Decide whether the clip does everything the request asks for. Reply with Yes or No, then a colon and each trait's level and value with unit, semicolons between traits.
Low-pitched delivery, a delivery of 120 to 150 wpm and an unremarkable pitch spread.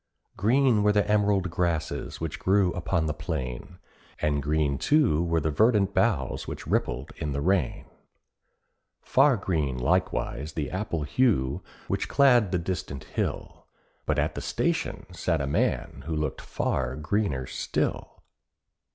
No: very low, 85 Hz; average, 145 wpm; wide, 5.8 semitones